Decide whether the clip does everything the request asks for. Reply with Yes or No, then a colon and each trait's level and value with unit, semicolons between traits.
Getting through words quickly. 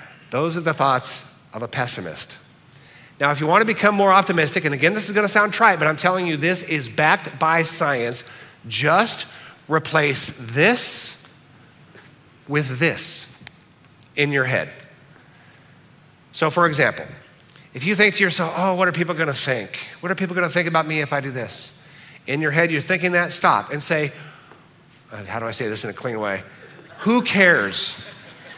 No: average, 185 wpm